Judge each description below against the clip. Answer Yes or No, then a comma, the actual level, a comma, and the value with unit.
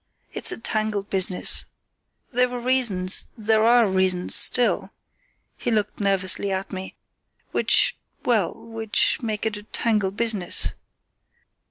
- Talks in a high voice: Yes, high, 215 Hz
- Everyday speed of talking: No, slow, 110 wpm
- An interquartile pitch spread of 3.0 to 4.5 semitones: Yes, average, 3.3 semitones